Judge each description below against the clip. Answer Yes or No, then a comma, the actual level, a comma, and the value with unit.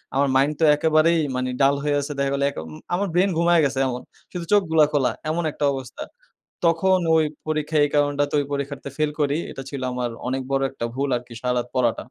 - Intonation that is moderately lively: Yes, average, 3.0 semitones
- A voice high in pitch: No, medium, 145 Hz